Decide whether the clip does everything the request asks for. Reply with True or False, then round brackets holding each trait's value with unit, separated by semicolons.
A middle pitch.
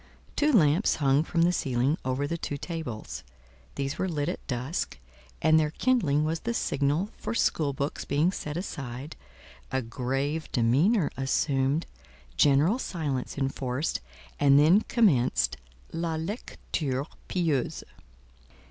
True (145 Hz)